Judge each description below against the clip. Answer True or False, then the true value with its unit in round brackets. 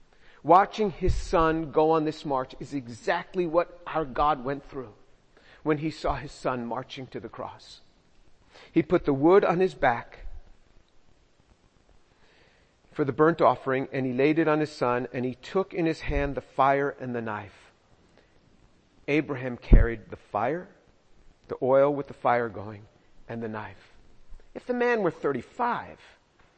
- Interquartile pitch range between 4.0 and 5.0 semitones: True (4.7 semitones)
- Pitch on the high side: False (140 Hz)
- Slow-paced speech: False (160 wpm)